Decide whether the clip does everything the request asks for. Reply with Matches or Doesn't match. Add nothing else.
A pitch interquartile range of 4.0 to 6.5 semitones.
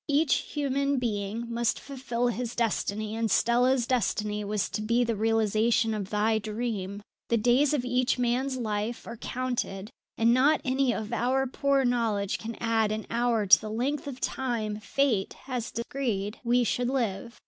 Doesn't match